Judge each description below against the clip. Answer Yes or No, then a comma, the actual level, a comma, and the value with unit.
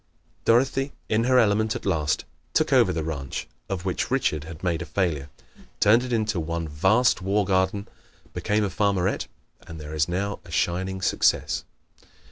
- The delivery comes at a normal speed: Yes, average, 165 wpm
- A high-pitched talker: No, very low, 95 Hz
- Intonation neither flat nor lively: Yes, average, 4.6 semitones